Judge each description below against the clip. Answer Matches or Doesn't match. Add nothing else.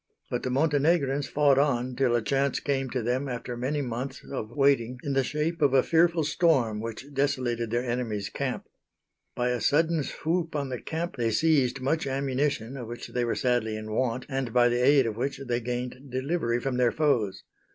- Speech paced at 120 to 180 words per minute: Doesn't match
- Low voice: Matches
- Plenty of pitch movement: Doesn't match